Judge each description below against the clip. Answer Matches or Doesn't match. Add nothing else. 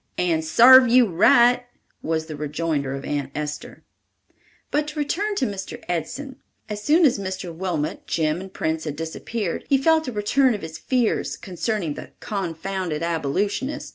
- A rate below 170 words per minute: Matches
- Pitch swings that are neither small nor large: Doesn't match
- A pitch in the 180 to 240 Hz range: Matches